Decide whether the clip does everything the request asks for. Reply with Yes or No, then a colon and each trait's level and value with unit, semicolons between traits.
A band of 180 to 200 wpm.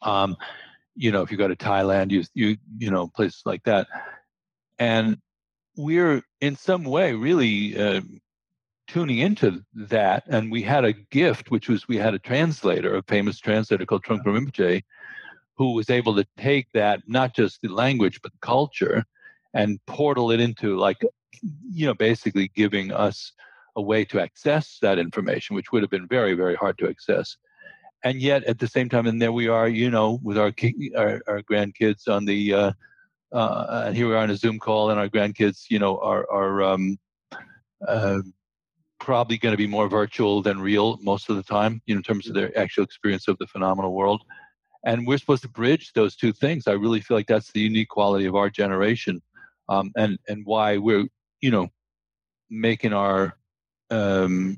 Yes: average, 190 wpm